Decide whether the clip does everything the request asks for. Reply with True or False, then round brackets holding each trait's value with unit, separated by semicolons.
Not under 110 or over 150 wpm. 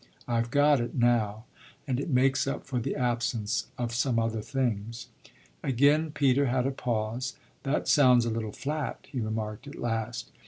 False (165 wpm)